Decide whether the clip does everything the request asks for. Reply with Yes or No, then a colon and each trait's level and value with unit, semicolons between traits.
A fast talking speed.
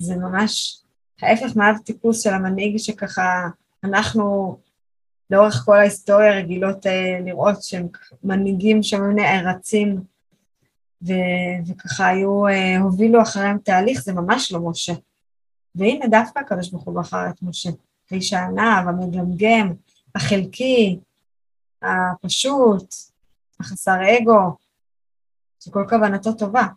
No: average, 105 wpm